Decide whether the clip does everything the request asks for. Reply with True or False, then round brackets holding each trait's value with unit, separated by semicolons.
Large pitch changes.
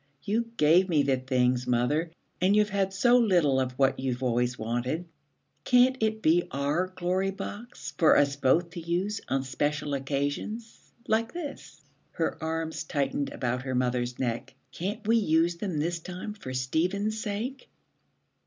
True (7.1 semitones)